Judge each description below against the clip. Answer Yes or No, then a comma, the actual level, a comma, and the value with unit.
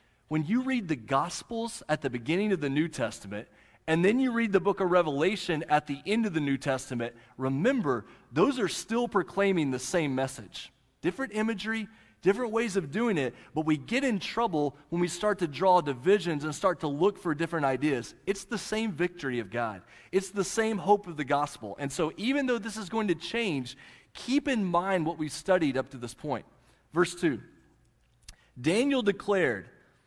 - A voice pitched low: No, medium, 175 Hz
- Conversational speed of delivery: Yes, average, 190 wpm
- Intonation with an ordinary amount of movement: No, wide, 6.8 semitones